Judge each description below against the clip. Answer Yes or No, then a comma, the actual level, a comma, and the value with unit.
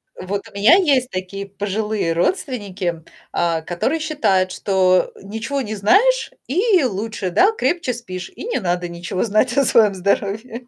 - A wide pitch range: Yes, wide, 5.7 semitones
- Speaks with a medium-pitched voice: No, high, 205 Hz